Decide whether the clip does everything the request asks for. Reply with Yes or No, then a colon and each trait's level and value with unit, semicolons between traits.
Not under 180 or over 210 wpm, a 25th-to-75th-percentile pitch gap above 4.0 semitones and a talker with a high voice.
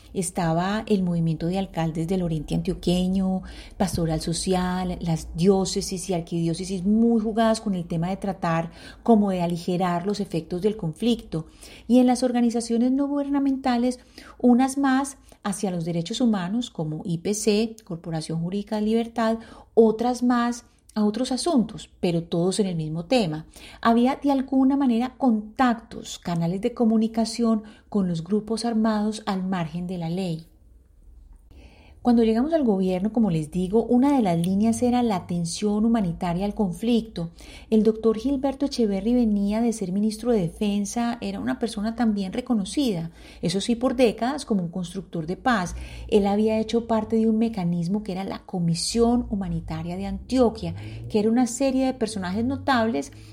No: average, 155 wpm; average, 4.8 semitones; high, 210 Hz